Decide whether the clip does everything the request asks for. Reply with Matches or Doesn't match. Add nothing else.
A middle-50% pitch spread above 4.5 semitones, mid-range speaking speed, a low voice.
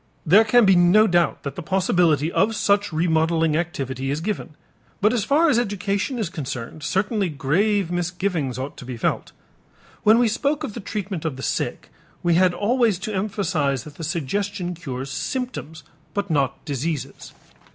Doesn't match